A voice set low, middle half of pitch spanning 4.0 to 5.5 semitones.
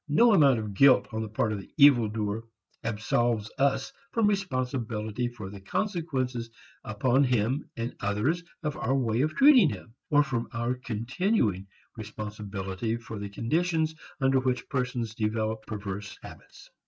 Yes: low, 120 Hz; average, 4.5 semitones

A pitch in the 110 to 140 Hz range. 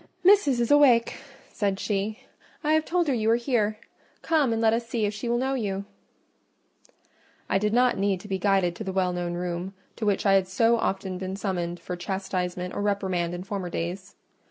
No: high, 200 Hz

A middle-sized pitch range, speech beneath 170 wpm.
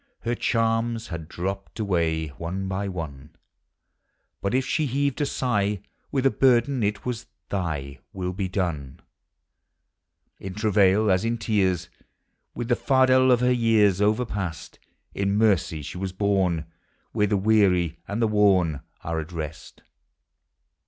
Yes: average, 4.4 semitones; average, 145 wpm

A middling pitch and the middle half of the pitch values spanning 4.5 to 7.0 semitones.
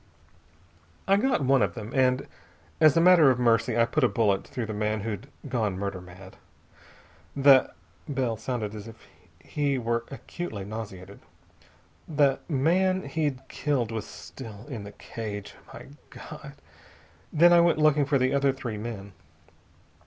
No: low, 125 Hz; average, 5.1 semitones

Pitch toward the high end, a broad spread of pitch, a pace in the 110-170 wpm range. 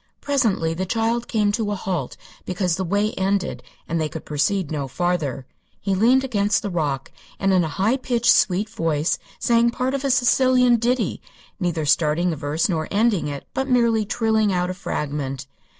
No: high, 195 Hz; wide, 6.2 semitones; average, 180 wpm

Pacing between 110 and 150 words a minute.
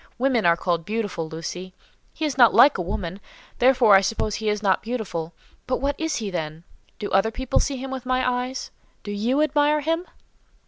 No: average, 195 wpm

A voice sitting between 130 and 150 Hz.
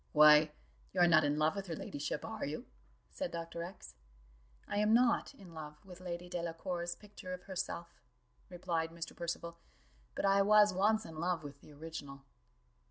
No: medium, 170 Hz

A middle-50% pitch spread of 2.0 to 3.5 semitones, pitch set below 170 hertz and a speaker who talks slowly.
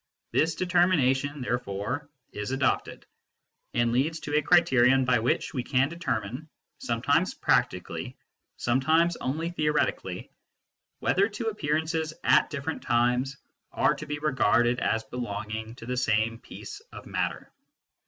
No: average, 4.8 semitones; low, 135 Hz; slow, 130 wpm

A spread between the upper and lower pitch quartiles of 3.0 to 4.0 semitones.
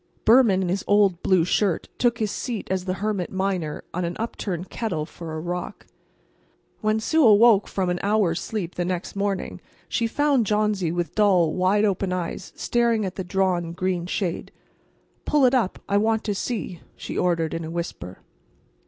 Yes: average, 3.4 semitones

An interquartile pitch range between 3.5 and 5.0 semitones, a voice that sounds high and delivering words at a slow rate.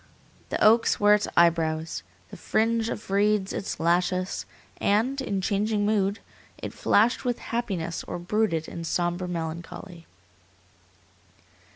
Yes: average, 3.8 semitones; high, 195 Hz; slow, 120 wpm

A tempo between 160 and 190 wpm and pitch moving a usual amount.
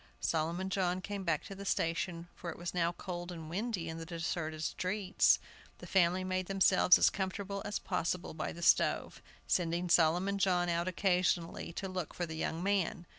No: average, 180 wpm; narrow, 2.1 semitones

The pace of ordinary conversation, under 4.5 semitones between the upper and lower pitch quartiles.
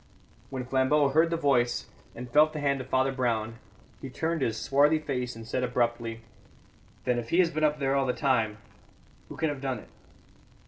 Yes: average, 195 wpm; average, 3.5 semitones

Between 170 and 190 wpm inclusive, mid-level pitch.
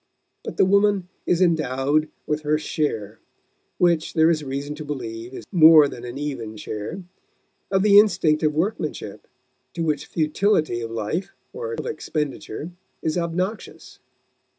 No: average, 145 wpm; medium, 155 Hz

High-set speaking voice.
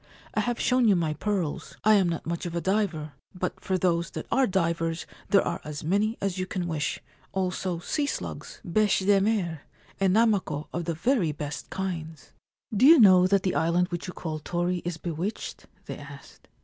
No: medium, 180 Hz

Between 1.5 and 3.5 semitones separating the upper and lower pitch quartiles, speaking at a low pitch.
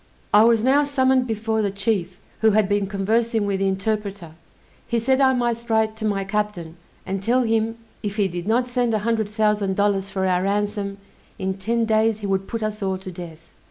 No: narrow, 2.6 semitones; high, 210 Hz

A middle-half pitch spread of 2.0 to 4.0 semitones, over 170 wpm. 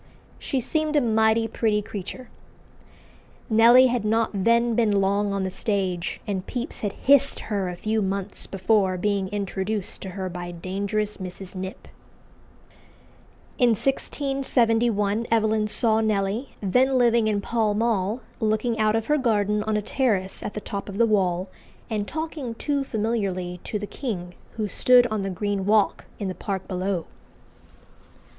No: average, 3.0 semitones; average, 155 wpm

